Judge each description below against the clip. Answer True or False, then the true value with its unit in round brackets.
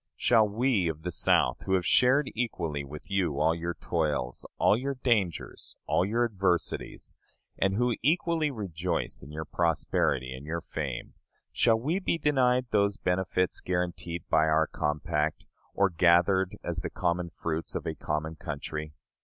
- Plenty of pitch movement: True (5.9 semitones)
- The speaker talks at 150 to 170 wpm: True (155 wpm)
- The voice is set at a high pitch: False (90 Hz)